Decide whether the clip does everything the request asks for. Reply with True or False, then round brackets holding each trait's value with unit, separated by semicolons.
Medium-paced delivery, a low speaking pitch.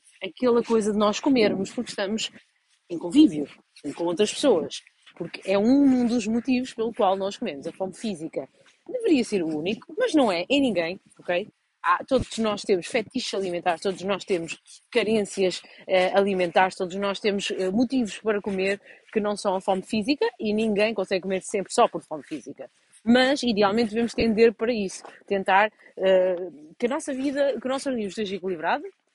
False (175 wpm; 210 Hz)